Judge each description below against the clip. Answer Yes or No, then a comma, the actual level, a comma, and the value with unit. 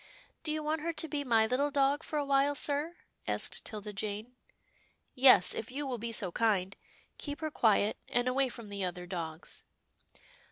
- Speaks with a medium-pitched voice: No, very high, 250 Hz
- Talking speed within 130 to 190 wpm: No, average, 200 wpm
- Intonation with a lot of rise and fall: Yes, wide, 5.7 semitones